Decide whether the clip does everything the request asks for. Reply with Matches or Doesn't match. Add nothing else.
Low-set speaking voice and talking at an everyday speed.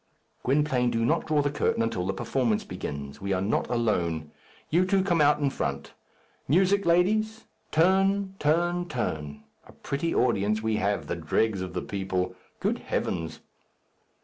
Matches